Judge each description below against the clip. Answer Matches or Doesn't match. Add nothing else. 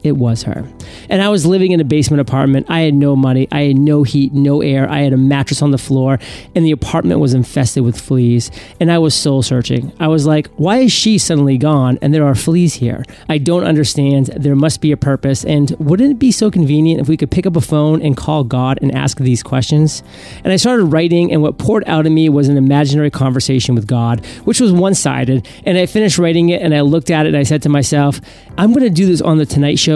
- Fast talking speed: Matches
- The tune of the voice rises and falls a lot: Doesn't match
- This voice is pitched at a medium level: Matches